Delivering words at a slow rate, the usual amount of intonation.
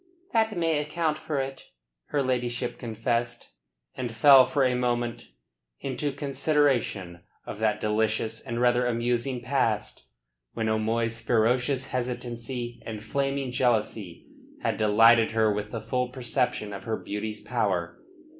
Yes: slow, 130 wpm; average, 3.0 semitones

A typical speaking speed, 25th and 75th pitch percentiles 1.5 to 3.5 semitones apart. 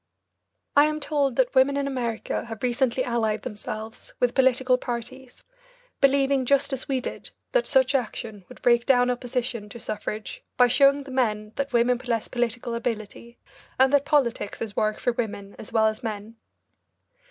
Yes: average, 165 wpm; average, 2.9 semitones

